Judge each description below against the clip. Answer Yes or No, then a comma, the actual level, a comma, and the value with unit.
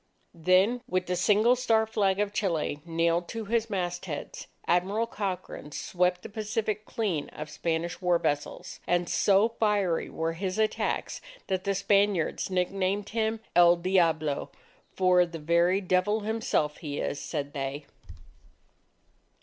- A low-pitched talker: No, medium, 185 Hz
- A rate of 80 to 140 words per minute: Yes, slow, 135 wpm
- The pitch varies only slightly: No, average, 3.6 semitones